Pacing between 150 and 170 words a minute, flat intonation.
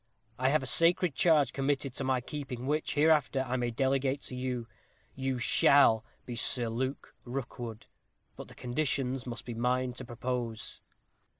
Yes: average, 160 wpm; narrow, 2.1 semitones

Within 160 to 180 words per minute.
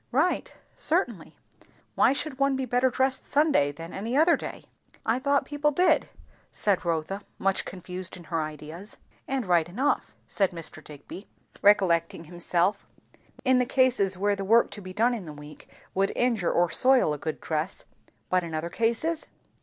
Yes: average, 170 wpm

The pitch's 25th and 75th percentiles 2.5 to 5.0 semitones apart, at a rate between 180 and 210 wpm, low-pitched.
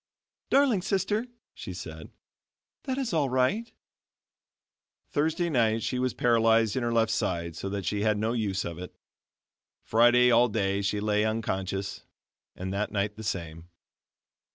No: average, 4.4 semitones; average, 150 wpm; low, 110 Hz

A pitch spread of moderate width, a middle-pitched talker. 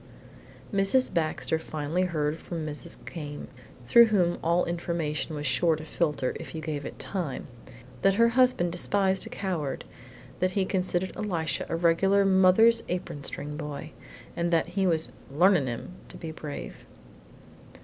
Yes: average, 3.6 semitones; medium, 170 Hz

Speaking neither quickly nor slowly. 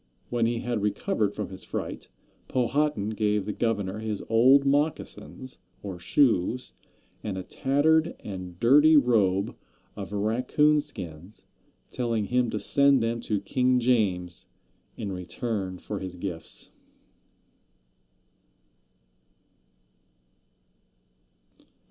No: slow, 105 wpm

